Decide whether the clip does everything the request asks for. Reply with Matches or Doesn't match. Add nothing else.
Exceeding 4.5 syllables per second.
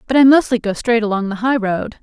Matches